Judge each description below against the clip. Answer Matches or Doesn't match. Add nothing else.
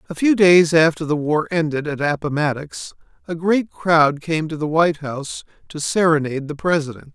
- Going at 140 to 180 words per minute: Matches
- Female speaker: Doesn't match